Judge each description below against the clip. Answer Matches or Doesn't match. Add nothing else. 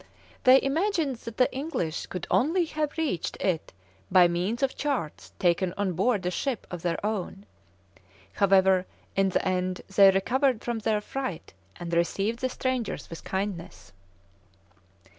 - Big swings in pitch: Matches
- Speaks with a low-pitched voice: Doesn't match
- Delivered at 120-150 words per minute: Matches